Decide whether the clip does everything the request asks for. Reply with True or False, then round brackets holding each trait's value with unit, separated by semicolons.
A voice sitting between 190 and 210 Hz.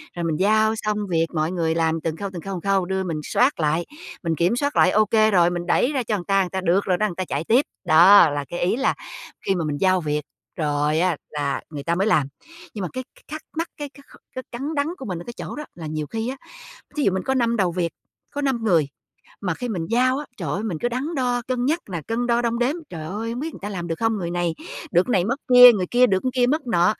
True (195 Hz)